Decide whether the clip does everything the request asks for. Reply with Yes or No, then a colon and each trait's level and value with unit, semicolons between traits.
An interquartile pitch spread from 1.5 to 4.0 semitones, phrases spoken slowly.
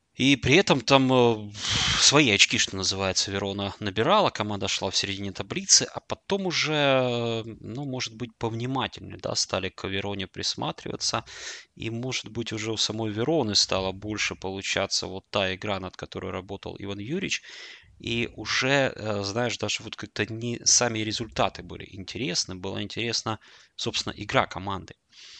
No: average, 3.6 semitones; average, 145 wpm